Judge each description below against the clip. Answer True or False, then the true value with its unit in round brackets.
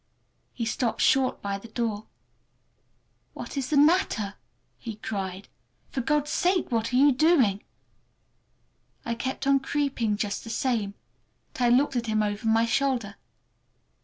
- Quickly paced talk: False (145 wpm)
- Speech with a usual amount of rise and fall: True (4.2 semitones)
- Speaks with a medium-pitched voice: False (235 Hz)